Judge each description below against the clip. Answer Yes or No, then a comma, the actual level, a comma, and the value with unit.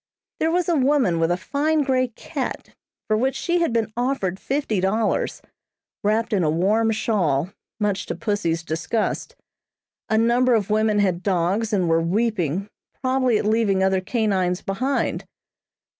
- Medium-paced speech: Yes, average, 155 wpm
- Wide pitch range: No, average, 4.6 semitones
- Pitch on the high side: Yes, high, 215 Hz